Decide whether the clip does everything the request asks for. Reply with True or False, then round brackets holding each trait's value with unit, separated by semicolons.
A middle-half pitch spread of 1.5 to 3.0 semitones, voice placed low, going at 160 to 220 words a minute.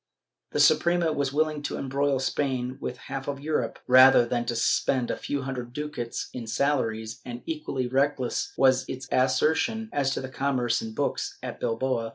True (2.7 semitones; 130 Hz; 180 wpm)